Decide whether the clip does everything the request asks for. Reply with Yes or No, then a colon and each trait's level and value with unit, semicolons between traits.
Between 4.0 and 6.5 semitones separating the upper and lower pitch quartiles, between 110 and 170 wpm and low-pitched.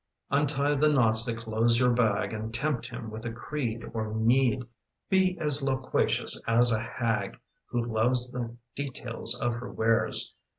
No: average, 2.9 semitones; average, 160 wpm; low, 120 Hz